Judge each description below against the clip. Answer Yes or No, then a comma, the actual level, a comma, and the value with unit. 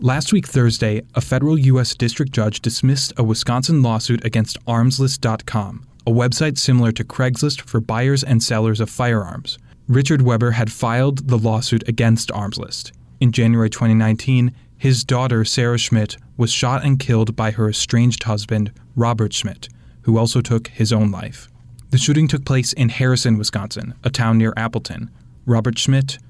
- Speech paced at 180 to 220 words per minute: No, average, 155 wpm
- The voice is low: Yes, low, 120 Hz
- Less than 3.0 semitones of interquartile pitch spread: Yes, narrow, 2.4 semitones